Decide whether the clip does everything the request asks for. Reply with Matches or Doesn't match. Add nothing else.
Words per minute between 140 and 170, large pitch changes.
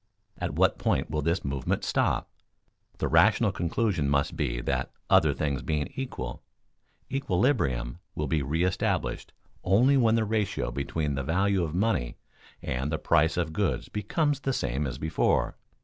Matches